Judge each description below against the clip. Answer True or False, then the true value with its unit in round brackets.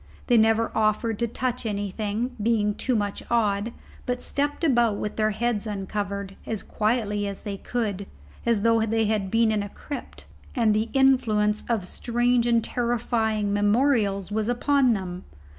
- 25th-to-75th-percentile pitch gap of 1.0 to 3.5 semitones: True (2.5 semitones)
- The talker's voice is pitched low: False (220 Hz)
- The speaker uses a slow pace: False (160 wpm)